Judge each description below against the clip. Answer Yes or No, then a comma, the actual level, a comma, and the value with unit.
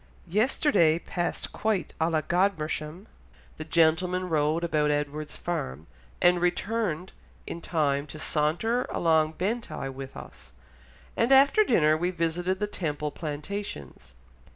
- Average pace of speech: No, slow, 125 wpm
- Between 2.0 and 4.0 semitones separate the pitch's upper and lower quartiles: Yes, average, 3.5 semitones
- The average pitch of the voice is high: No, medium, 165 Hz